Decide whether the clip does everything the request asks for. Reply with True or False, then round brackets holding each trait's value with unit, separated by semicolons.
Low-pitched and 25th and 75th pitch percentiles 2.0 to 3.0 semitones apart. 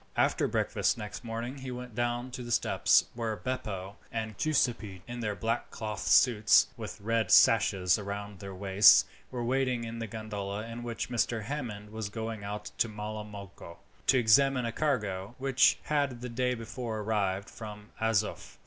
True (110 Hz; 2.7 semitones)